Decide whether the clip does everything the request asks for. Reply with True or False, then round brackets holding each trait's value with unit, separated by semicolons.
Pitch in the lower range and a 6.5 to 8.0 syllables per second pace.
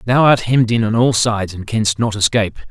False (110 Hz; 6.0 syllables/s)